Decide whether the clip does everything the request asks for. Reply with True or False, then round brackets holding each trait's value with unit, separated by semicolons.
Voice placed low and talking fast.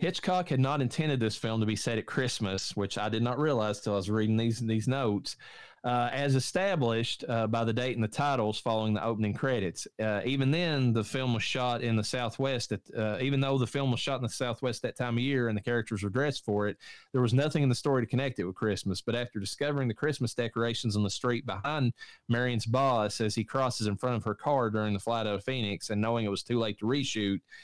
True (120 Hz; 245 wpm)